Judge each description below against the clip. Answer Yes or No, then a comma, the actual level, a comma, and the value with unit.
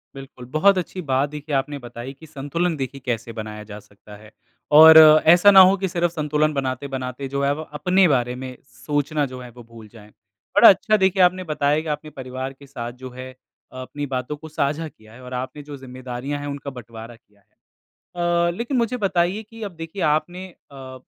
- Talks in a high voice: No, medium, 140 Hz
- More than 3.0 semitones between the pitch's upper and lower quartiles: Yes, average, 4.1 semitones